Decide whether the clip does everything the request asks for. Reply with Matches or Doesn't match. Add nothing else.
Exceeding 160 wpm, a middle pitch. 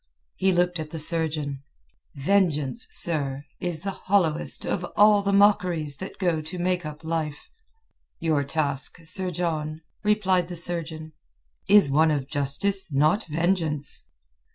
Doesn't match